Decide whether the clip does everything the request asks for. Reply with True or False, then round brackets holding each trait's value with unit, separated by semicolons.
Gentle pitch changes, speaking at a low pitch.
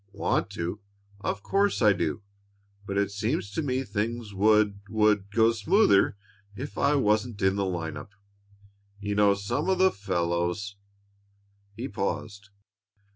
True (2.3 semitones; 100 Hz)